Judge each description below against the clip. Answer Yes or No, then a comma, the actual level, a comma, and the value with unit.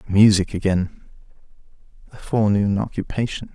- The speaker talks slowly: Yes, slow, 85 wpm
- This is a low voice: Yes, low, 100 Hz